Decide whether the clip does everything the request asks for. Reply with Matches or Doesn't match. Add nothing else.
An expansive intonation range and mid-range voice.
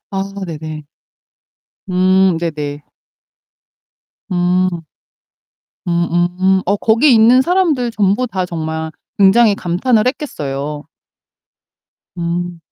Doesn't match